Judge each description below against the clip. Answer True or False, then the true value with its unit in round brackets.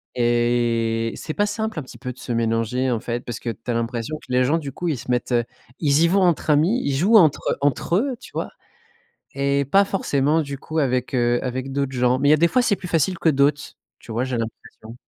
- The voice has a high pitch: False (135 Hz)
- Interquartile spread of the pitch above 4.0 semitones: True (4.9 semitones)